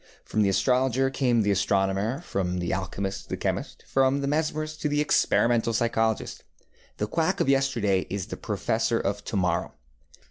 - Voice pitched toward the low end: Yes, low, 115 Hz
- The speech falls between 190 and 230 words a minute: No, average, 155 wpm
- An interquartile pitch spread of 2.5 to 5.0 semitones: No, wide, 5.4 semitones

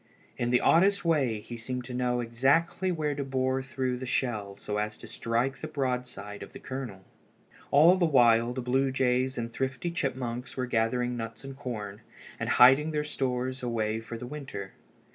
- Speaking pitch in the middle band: No, low, 125 Hz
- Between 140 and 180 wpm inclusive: No, average, 190 wpm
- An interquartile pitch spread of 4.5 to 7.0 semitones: No, narrow, 2.5 semitones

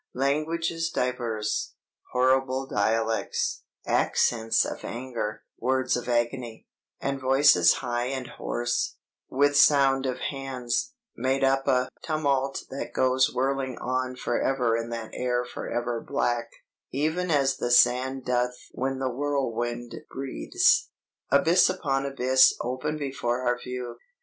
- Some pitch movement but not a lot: No, narrow, 2.1 semitones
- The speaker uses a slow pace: Yes, slow, 125 wpm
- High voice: No, low, 130 Hz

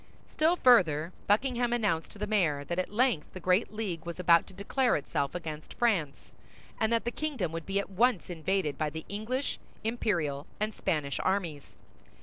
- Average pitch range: No, wide, 6.0 semitones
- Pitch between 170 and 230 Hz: Yes, high, 190 Hz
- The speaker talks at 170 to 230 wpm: Yes, average, 175 wpm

